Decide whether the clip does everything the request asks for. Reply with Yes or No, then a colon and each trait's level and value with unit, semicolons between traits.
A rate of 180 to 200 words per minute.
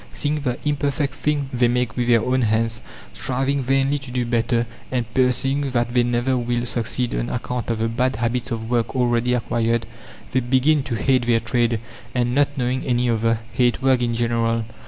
Yes: average, 190 wpm